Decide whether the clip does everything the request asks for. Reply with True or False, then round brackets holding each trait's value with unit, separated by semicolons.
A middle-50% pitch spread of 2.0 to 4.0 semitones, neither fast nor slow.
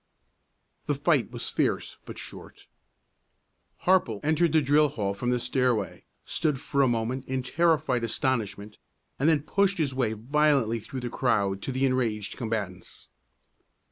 False (4.6 semitones; 145 wpm)